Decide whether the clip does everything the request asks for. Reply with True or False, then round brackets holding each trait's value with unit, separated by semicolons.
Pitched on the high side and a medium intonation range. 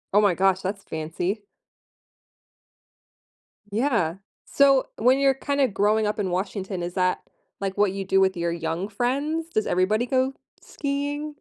False (205 Hz; 6.1 semitones)